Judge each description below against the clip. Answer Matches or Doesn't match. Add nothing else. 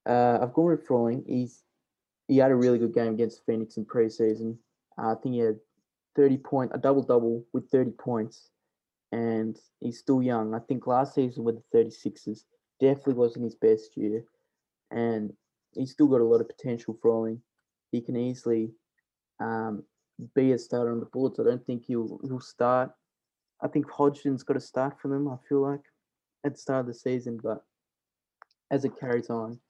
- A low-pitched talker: Matches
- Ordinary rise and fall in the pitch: Matches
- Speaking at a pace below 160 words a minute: Doesn't match